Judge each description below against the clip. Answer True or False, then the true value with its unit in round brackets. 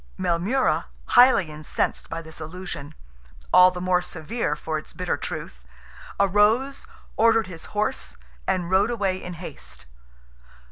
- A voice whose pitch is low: False (180 Hz)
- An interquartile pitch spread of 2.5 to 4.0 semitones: False (5.2 semitones)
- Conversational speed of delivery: False (120 wpm)